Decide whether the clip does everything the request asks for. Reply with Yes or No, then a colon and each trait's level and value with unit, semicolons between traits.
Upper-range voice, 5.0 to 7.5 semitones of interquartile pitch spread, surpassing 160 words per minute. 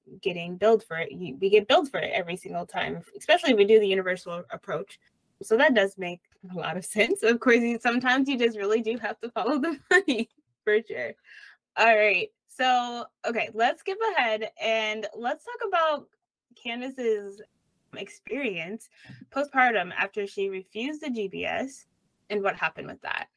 Yes: high, 225 Hz; wide, 5.4 semitones; average, 170 wpm